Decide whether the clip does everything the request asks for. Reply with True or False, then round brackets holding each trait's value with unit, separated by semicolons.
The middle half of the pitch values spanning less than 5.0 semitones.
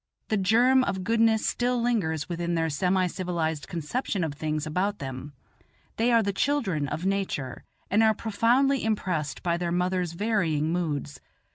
False (5.6 semitones)